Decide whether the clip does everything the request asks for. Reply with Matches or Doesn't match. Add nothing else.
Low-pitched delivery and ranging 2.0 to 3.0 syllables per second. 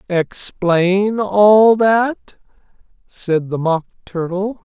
Doesn't match